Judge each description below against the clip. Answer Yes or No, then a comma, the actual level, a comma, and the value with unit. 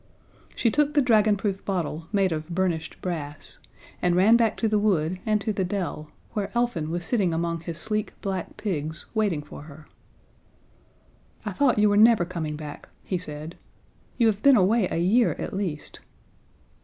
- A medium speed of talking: Yes, average, 170 wpm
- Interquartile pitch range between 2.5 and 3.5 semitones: No, average, 4.6 semitones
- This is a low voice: No, high, 190 Hz